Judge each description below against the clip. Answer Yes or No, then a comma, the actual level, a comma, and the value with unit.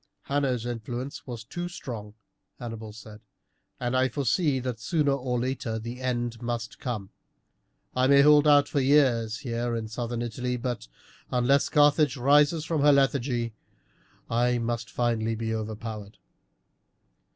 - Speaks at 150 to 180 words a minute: No, average, 140 wpm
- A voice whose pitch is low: Yes, low, 120 Hz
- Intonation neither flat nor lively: Yes, average, 3.3 semitones